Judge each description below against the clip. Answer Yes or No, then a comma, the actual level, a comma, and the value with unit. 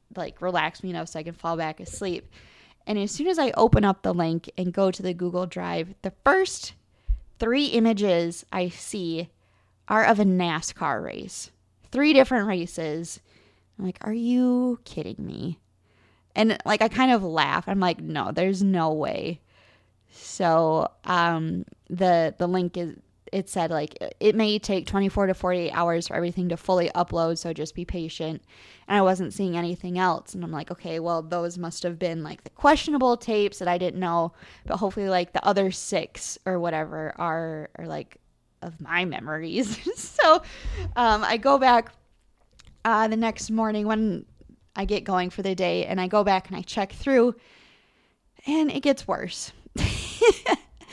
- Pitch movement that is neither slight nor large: Yes, average, 4.4 semitones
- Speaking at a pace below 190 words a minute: Yes, average, 175 wpm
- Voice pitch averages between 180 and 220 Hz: Yes, medium, 185 Hz